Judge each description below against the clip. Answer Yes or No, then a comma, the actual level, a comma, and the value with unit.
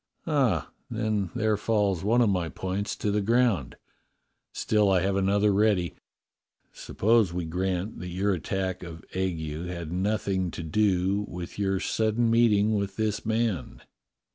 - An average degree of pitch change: Yes, average, 3.1 semitones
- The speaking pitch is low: Yes, low, 100 Hz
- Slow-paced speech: No, average, 145 wpm